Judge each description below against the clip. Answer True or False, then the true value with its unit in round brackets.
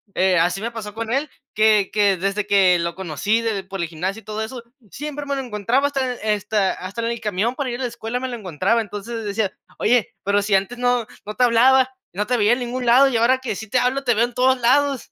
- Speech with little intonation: False (3.7 semitones)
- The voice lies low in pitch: False (225 Hz)